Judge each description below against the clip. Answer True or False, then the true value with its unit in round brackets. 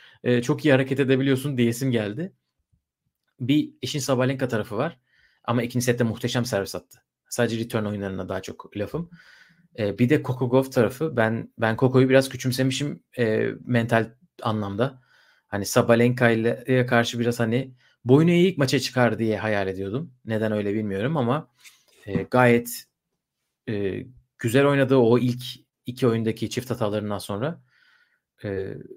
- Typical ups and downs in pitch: True (3.1 semitones)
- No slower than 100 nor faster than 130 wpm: False (140 wpm)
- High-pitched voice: False (125 Hz)